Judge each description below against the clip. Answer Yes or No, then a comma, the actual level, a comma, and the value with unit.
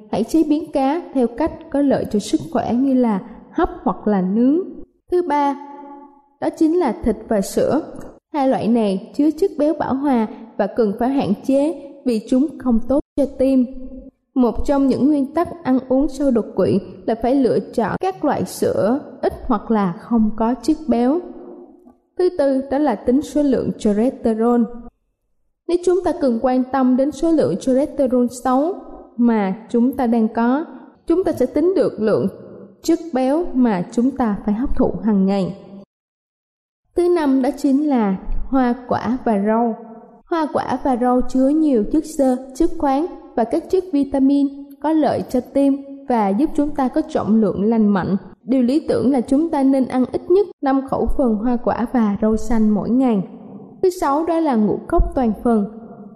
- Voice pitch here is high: Yes, very high, 260 Hz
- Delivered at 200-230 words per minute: No, average, 185 wpm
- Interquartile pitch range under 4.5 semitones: Yes, average, 3.9 semitones